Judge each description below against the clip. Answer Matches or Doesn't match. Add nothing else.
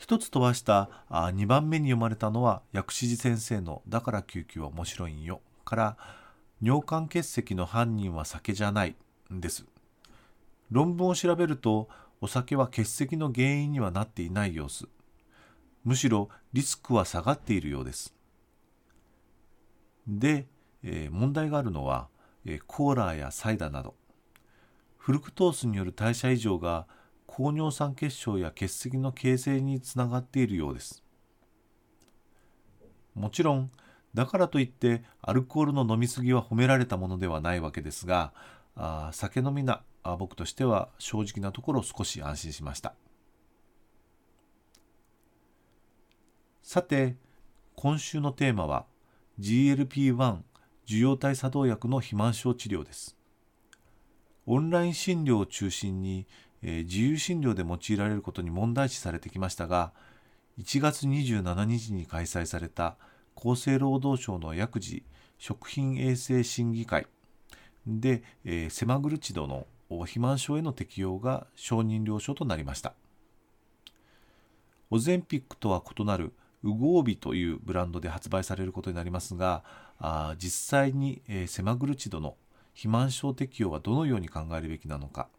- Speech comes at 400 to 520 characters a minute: Doesn't match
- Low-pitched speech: Matches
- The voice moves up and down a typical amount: Doesn't match